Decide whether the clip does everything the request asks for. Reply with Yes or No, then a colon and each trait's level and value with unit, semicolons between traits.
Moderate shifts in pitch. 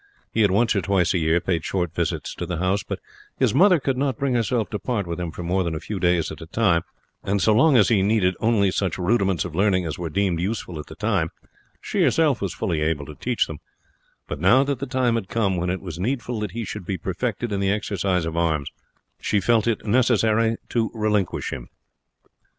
Yes: average, 4.6 semitones